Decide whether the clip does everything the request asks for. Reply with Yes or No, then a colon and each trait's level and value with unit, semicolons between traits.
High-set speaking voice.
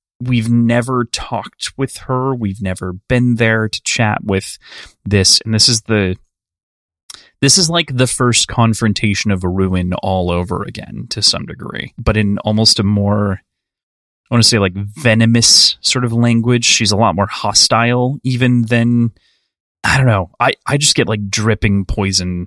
No: low, 110 Hz